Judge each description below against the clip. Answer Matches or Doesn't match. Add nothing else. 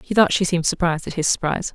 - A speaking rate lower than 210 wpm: Doesn't match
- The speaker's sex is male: Doesn't match